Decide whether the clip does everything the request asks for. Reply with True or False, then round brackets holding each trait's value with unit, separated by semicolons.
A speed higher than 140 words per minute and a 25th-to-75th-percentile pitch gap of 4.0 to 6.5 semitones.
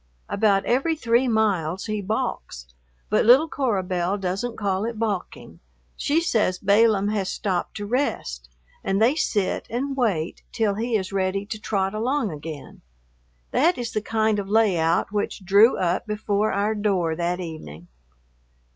False (155 wpm; 3.2 semitones)